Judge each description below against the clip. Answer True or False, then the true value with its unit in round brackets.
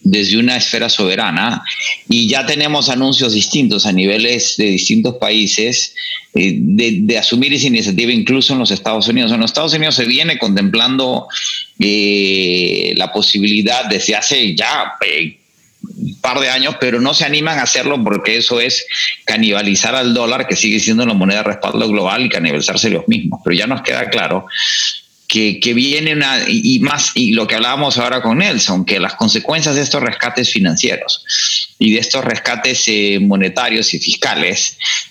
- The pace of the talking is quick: False (170 wpm)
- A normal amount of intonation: False (6.5 semitones)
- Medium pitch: False (125 Hz)